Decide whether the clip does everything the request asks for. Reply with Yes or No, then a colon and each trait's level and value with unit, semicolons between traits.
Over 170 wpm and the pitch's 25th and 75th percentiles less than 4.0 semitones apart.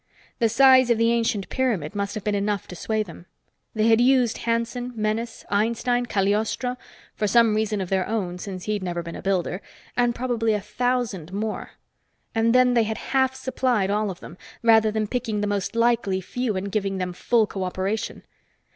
Yes: average, 180 wpm; average, 3.1 semitones